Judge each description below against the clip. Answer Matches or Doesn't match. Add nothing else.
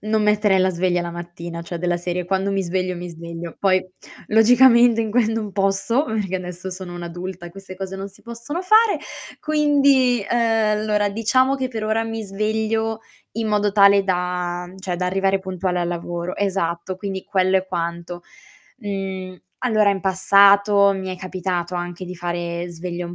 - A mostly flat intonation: Doesn't match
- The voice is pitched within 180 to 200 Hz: Matches